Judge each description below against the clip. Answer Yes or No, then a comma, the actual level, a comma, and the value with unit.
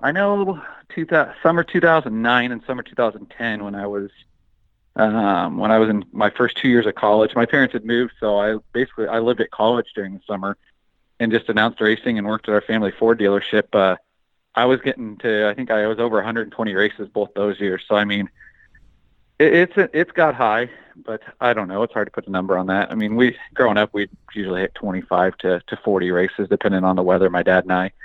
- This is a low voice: Yes, low, 110 Hz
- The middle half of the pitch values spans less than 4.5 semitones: Yes, average, 3.4 semitones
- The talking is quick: Yes, fast, 220 wpm